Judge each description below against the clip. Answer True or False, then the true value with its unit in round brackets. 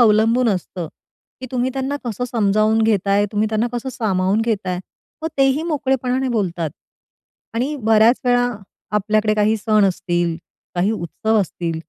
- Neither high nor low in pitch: False (220 Hz)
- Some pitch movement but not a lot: True (3.7 semitones)